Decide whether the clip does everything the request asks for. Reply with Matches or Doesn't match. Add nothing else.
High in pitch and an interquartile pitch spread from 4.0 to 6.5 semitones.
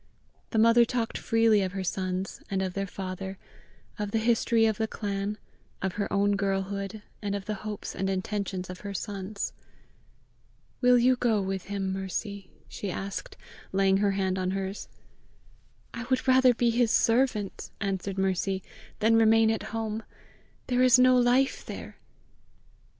Doesn't match